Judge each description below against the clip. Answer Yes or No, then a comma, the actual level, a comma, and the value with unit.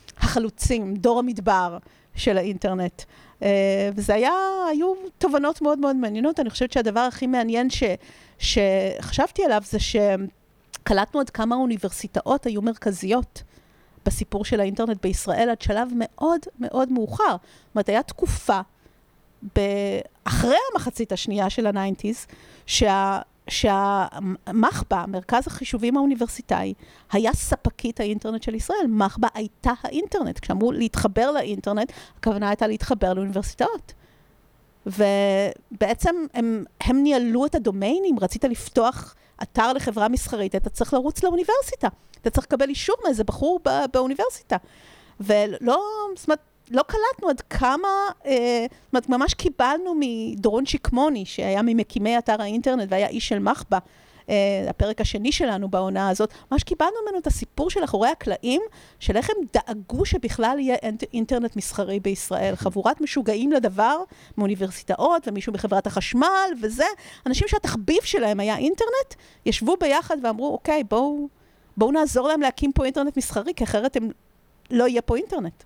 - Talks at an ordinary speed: Yes, average, 130 wpm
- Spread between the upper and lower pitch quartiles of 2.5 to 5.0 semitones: No, wide, 5.5 semitones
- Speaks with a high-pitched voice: Yes, high, 235 Hz